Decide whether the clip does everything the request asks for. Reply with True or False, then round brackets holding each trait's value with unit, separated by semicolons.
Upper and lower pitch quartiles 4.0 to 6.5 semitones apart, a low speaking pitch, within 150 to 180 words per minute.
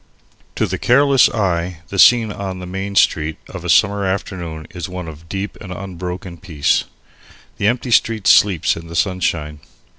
False (3.0 semitones; 95 Hz; 170 wpm)